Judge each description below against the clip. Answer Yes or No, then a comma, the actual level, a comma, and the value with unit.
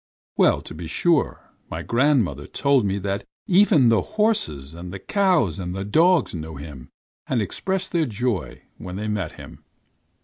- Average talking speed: Yes, average, 165 wpm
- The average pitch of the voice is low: Yes, low, 105 Hz